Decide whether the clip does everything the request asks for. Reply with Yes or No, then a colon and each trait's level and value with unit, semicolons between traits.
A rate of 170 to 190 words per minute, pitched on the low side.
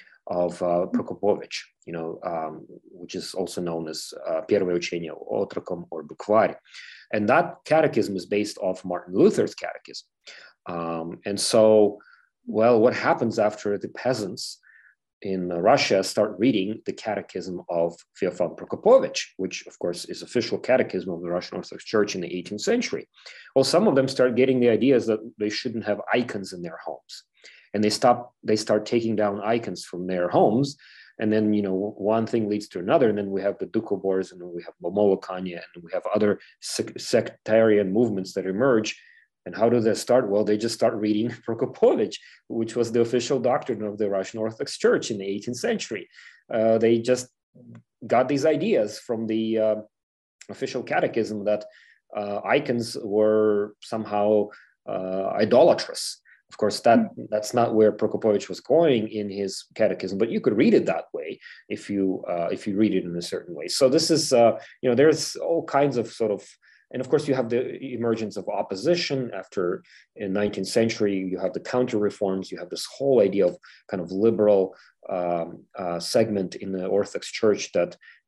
Yes: average, 175 wpm; low, 105 Hz